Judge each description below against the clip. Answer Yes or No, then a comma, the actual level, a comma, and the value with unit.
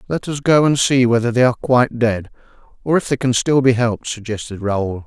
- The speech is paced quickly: Yes, fast, 225 wpm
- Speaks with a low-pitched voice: Yes, low, 120 Hz